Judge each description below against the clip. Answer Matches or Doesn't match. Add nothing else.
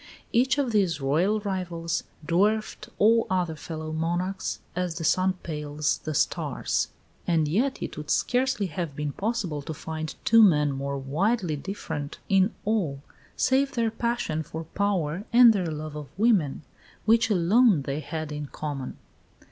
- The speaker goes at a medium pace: Matches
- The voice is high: Doesn't match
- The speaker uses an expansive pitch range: Matches